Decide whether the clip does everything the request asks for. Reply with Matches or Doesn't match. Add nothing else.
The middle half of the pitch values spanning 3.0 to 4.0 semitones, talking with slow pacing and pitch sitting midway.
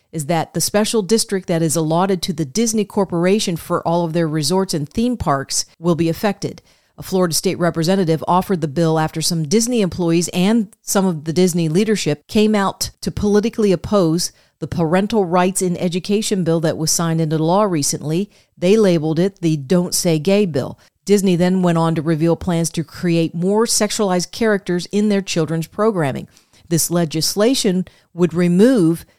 Doesn't match